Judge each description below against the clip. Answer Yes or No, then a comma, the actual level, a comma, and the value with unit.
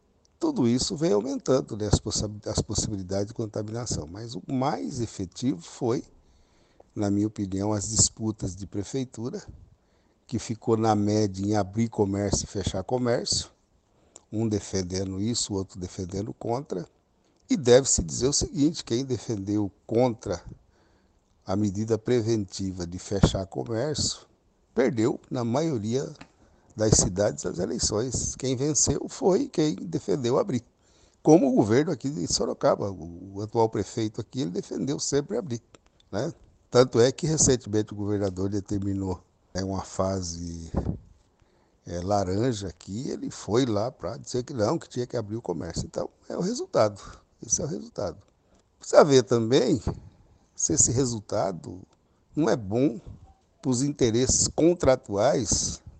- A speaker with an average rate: Yes, average, 140 wpm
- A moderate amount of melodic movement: Yes, average, 4.0 semitones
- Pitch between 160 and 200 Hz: No, low, 105 Hz